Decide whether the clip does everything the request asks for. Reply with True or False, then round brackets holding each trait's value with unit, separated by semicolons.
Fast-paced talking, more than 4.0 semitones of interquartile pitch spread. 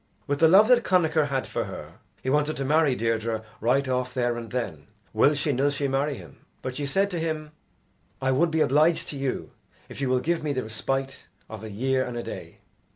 False (220 wpm; 3.5 semitones)